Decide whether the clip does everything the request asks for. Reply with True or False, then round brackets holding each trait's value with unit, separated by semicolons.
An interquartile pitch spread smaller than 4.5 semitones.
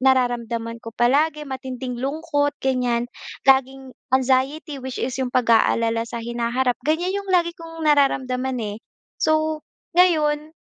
True (3.9 semitones)